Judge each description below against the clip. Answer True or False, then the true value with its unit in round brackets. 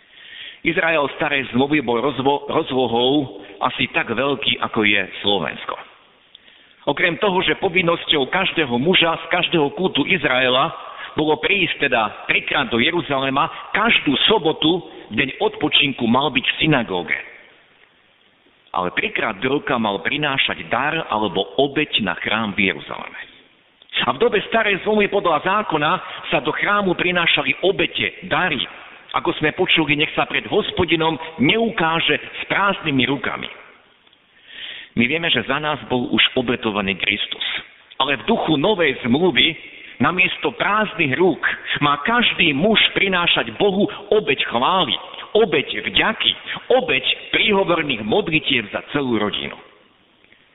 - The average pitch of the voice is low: False (155 Hz)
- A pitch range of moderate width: False (5.8 semitones)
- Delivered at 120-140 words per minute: True (125 wpm)